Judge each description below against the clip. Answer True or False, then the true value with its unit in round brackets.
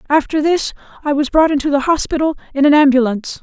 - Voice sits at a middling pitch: False (290 Hz)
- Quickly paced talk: False (195 wpm)